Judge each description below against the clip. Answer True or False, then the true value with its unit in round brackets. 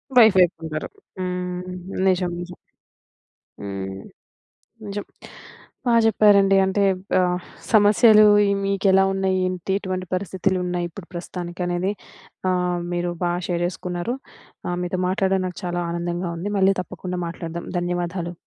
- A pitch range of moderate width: False (1.7 semitones)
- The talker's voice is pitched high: False (180 Hz)